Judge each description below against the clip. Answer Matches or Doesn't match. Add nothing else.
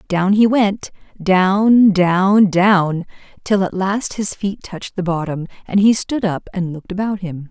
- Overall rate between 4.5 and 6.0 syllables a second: Doesn't match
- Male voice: Doesn't match